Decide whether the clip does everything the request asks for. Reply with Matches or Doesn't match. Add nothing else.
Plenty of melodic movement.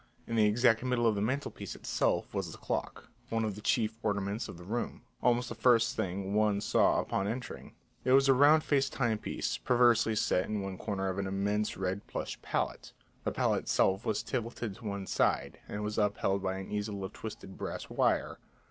Doesn't match